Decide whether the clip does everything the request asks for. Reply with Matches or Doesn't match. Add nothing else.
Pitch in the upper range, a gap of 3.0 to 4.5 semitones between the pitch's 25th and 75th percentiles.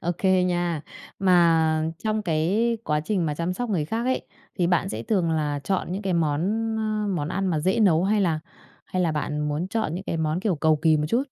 Doesn't match